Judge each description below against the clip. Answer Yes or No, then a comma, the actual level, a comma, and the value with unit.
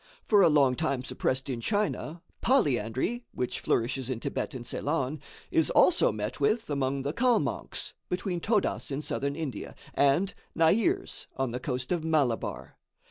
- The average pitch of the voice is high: No, medium, 140 Hz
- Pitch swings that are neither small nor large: No, wide, 5.8 semitones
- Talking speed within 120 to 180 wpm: Yes, average, 150 wpm